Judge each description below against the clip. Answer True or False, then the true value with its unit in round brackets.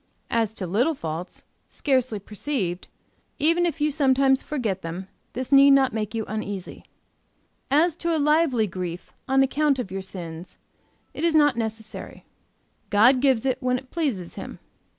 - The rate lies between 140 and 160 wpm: True (150 wpm)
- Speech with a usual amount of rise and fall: False (6.2 semitones)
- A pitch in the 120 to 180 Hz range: False (250 Hz)